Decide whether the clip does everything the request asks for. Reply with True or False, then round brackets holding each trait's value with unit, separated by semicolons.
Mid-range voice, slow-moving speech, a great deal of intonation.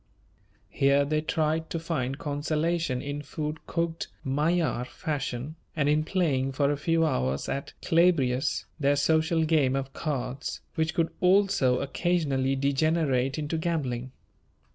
False (150 Hz; 130 wpm; 3.1 semitones)